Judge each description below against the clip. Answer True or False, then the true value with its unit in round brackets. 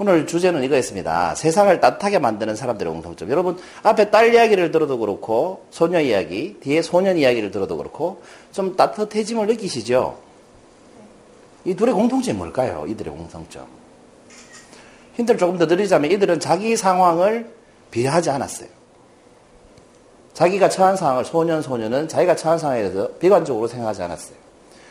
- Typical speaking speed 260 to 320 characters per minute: False (365 characters per minute)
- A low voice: False (180 Hz)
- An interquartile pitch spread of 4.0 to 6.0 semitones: True (5.3 semitones)